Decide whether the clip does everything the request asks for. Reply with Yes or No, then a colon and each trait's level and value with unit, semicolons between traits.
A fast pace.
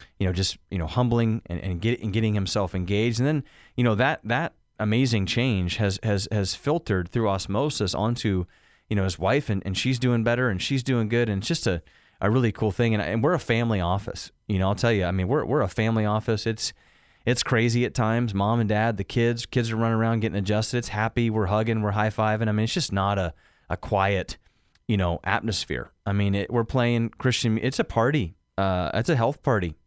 Yes: fast, 230 wpm